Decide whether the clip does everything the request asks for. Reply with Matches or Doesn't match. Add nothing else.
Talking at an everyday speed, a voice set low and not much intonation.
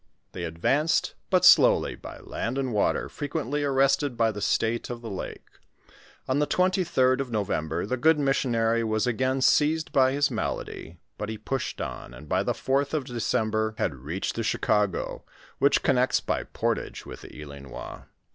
Doesn't match